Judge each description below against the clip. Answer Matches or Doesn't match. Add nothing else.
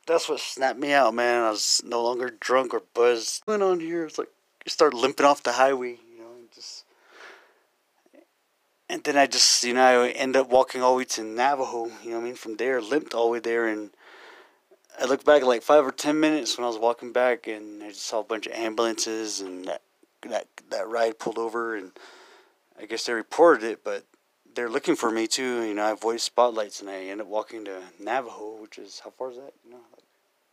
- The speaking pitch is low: Matches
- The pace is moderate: Doesn't match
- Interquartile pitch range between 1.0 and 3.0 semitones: Matches